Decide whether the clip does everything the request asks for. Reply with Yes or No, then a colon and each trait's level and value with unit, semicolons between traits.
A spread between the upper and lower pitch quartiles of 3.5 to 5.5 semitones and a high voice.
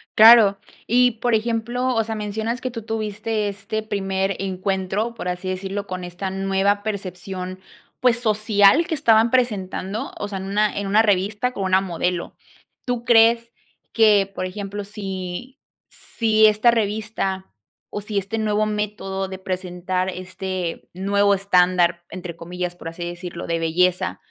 No: average, 2.8 semitones; high, 200 Hz